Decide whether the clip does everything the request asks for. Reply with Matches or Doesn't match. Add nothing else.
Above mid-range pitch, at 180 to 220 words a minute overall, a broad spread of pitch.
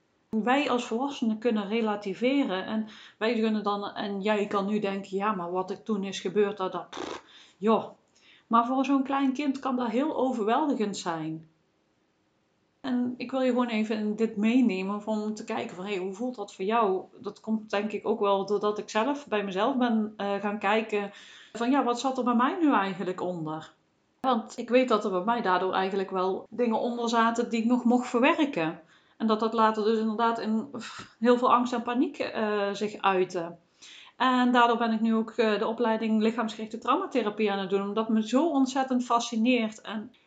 Doesn't match